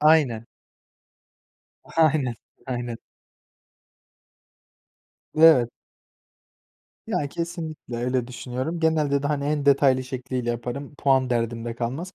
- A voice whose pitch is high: No, low, 135 Hz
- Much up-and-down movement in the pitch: No, average, 3.8 semitones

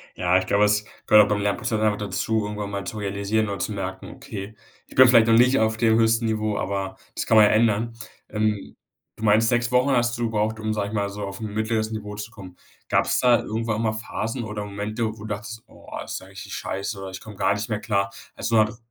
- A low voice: Yes, low, 110 Hz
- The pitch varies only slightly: Yes, narrow, 1.8 semitones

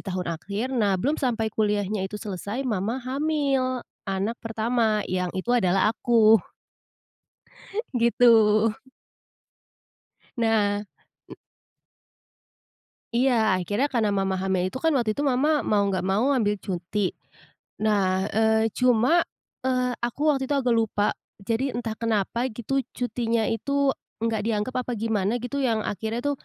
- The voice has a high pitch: Yes, high, 225 Hz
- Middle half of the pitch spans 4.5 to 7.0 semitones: No, average, 3.5 semitones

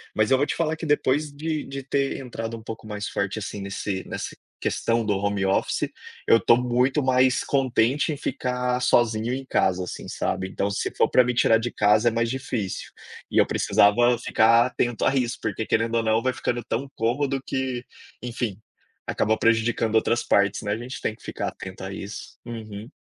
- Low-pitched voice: Yes, low, 115 Hz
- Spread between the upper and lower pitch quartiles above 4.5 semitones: No, average, 3.0 semitones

